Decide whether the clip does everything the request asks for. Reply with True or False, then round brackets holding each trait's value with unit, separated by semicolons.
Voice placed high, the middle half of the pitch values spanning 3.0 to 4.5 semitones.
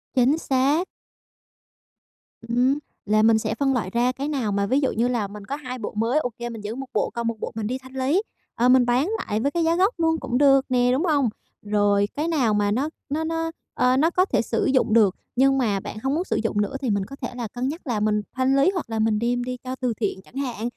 True (250 Hz; 3.8 semitones)